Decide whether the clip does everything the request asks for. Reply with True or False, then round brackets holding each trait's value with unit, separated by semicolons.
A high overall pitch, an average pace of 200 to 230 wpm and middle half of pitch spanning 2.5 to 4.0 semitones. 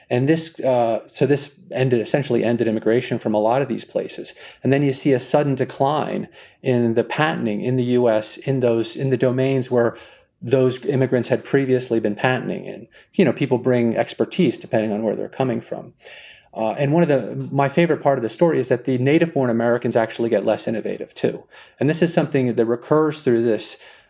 False (130 Hz; 205 wpm; 2.9 semitones)